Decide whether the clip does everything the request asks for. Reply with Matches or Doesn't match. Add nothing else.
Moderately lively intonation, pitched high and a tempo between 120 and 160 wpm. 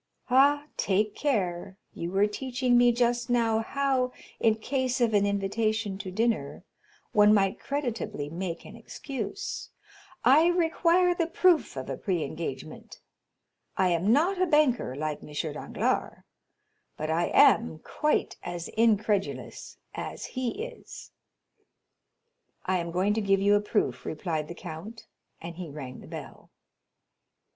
Doesn't match